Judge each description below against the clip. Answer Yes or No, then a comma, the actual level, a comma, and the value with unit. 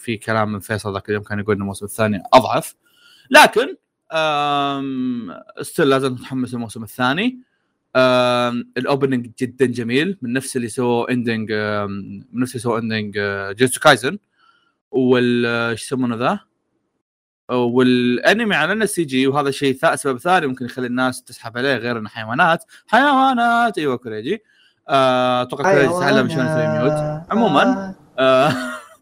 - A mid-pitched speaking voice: No, low, 125 Hz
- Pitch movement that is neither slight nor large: Yes, average, 3.4 semitones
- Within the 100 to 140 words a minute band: Yes, average, 130 wpm